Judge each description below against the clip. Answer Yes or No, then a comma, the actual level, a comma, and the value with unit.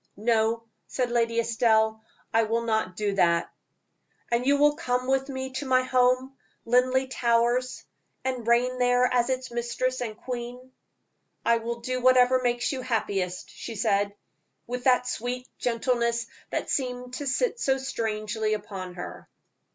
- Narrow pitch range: Yes, narrow, 2.1 semitones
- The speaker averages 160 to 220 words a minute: No, average, 150 wpm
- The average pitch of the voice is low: No, high, 245 Hz